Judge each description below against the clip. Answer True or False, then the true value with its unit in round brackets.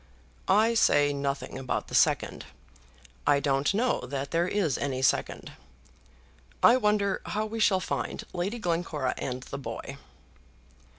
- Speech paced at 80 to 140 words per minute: True (135 wpm)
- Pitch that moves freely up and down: True (7.1 semitones)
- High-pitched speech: False (165 Hz)